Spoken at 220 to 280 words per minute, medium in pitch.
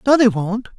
No: fast, 230 wpm; high, 225 Hz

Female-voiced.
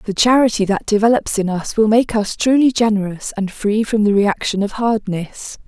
Yes: female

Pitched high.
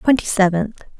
Yes: high, 205 Hz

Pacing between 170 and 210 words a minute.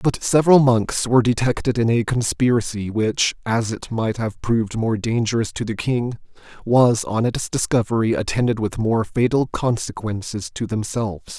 No: average, 160 wpm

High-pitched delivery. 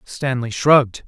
No: low, 125 Hz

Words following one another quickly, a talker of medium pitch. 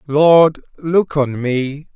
No: slow, 125 wpm; medium, 145 Hz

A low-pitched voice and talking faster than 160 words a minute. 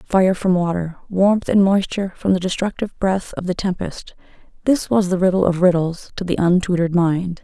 No: medium, 185 Hz; average, 185 wpm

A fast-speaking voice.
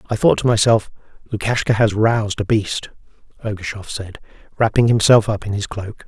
No: average, 170 wpm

